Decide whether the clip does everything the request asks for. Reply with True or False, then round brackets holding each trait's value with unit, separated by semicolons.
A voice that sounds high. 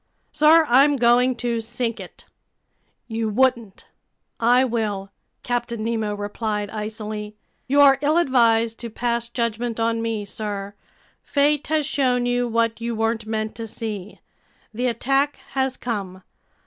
True (230 Hz)